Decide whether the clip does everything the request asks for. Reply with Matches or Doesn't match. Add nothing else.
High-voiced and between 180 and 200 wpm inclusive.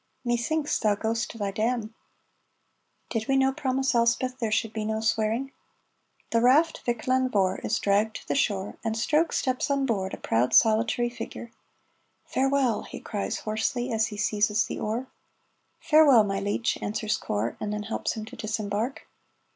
Doesn't match